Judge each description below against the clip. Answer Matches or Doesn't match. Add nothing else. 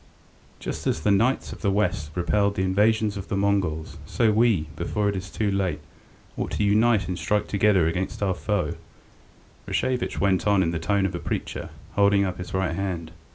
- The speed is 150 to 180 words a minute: Doesn't match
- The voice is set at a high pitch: Doesn't match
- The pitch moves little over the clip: Matches